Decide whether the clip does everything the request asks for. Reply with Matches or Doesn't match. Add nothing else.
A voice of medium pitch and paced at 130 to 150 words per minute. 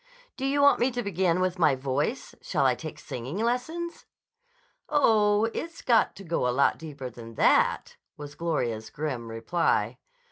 Doesn't match